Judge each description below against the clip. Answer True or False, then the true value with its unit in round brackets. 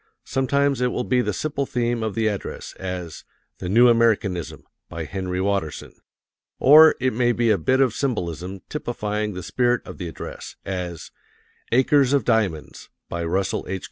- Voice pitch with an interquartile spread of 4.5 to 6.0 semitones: True (5.3 semitones)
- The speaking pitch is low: True (110 Hz)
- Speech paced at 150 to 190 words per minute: True (165 wpm)